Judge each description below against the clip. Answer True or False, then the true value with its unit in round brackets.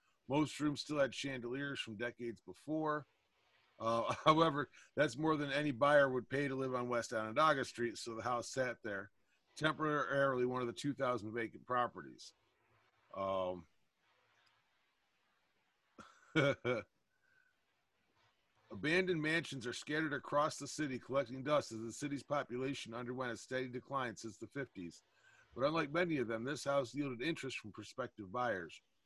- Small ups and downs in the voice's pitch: False (3.6 semitones)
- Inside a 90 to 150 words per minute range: True (140 wpm)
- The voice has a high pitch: False (135 Hz)